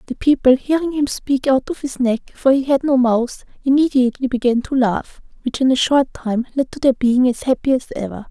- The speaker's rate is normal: No, fast, 225 wpm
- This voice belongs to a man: No, female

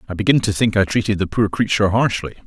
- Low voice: Yes, low, 105 Hz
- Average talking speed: No, fast, 245 wpm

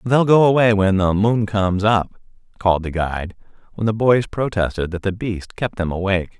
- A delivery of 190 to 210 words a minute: Yes, average, 195 wpm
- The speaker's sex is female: No, male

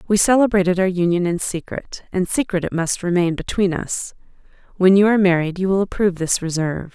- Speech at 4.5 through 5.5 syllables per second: No, 5.9 syllables/s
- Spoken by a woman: Yes, female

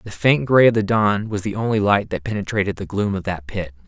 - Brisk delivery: Yes, fast, 265 wpm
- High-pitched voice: No, low, 105 Hz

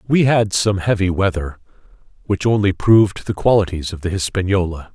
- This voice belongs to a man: Yes, male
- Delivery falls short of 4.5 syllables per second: No, 5.4 syllables/s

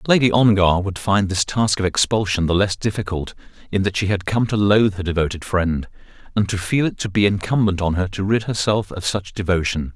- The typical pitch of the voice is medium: No, low, 100 Hz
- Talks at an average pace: No, fast, 215 wpm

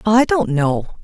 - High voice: Yes, high, 200 Hz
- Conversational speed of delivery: Yes, average, 175 wpm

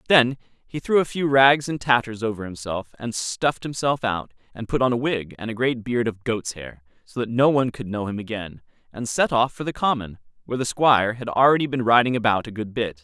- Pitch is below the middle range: Yes, low, 120 Hz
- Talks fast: Yes, fast, 235 wpm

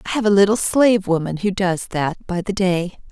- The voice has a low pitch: No, high, 190 Hz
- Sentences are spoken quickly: Yes, fast, 230 wpm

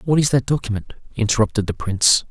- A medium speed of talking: Yes, average, 180 wpm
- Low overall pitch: Yes, low, 120 Hz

